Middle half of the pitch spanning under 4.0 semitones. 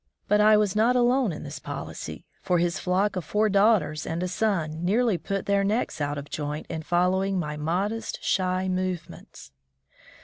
No: average, 4.5 semitones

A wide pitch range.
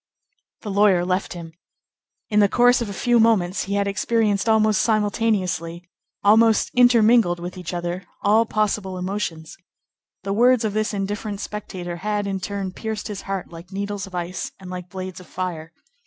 No: average, 2.8 semitones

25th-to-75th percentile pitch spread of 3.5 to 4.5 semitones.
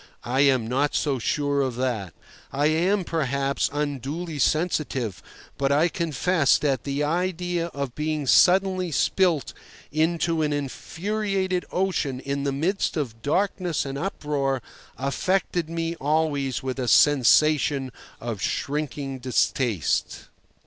Yes: average, 3.8 semitones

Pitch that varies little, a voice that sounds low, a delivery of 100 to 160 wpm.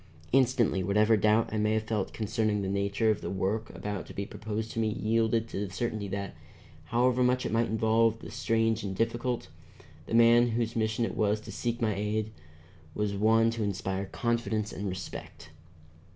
No: narrow, 1.9 semitones; low, 110 Hz; average, 190 wpm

